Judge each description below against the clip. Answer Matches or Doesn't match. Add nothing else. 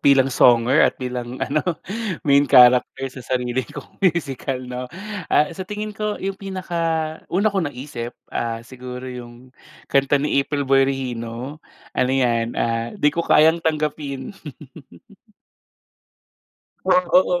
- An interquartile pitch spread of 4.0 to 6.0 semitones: Matches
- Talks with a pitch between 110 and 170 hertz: Matches